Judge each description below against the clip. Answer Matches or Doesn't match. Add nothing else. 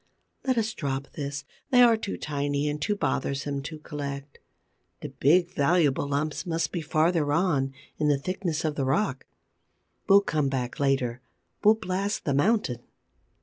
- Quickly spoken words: Doesn't match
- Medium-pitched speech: Matches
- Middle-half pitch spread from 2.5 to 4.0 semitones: Doesn't match